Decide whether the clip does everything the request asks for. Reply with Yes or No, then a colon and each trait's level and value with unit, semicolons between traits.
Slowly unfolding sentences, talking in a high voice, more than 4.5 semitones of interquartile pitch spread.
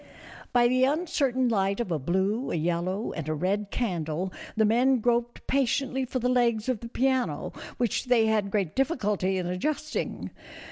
No: average, 170 wpm; high, 230 Hz; average, 5.1 semitones